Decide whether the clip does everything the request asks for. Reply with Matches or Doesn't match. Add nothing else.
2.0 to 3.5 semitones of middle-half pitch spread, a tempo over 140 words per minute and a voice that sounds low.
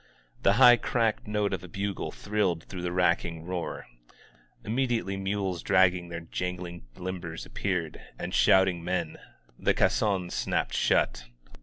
Doesn't match